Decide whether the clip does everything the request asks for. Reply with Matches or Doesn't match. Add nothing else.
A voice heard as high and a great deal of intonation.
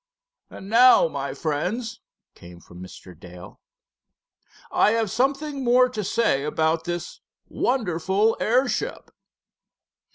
Matches